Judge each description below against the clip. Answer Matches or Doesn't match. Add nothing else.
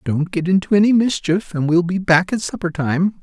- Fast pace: Matches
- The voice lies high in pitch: Doesn't match